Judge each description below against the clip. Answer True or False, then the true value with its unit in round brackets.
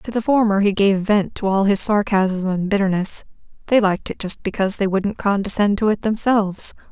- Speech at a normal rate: False (210 wpm)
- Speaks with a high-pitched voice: True (200 Hz)